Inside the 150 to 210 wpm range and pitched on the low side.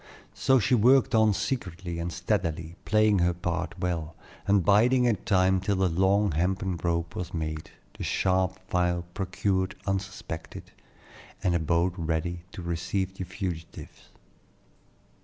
No: average, 140 wpm; very low, 90 Hz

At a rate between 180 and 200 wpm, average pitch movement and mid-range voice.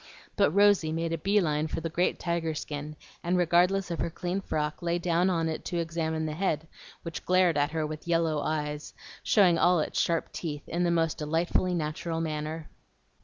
No: average, 195 wpm; narrow, 2.1 semitones; medium, 165 Hz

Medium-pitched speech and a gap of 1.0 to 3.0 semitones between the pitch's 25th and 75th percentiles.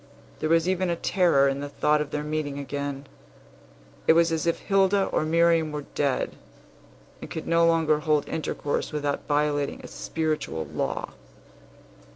Yes: medium, 155 Hz; narrow, 2.6 semitones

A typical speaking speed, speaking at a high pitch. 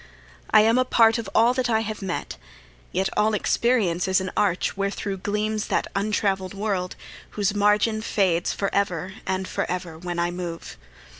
Yes: average, 165 wpm; high, 200 Hz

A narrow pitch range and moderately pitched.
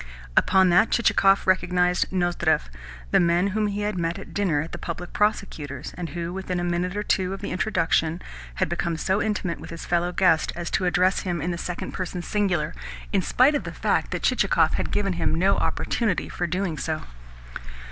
Yes: narrow, 2.3 semitones; medium, 180 Hz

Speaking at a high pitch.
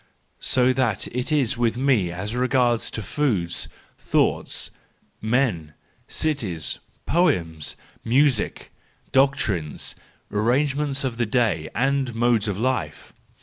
No: low, 120 Hz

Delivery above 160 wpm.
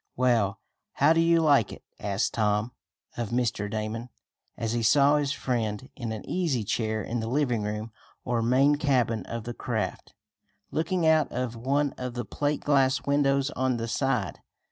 Yes: average, 170 wpm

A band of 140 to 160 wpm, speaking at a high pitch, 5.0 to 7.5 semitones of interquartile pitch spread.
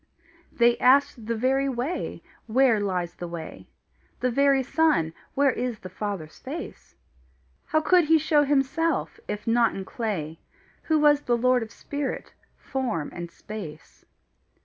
Yes: average, 145 wpm; high, 245 Hz; wide, 5.6 semitones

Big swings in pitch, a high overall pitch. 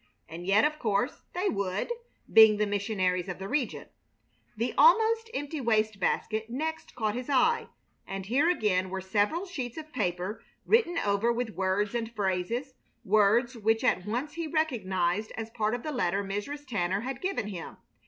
Yes: wide, 5.7 semitones; high, 220 Hz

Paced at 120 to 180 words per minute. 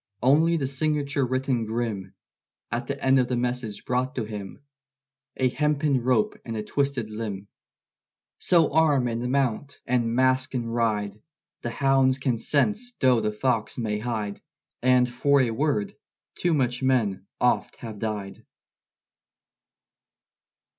Yes: average, 140 wpm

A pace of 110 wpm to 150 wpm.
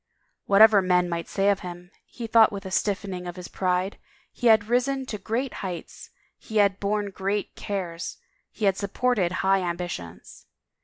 No: average, 165 wpm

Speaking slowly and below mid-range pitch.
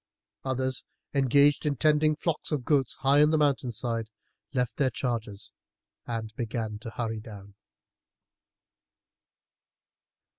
Yes: slow, 120 wpm; low, 130 Hz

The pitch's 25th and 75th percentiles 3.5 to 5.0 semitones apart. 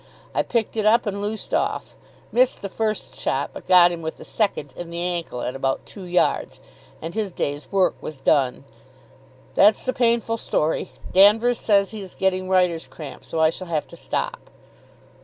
Yes: average, 4.7 semitones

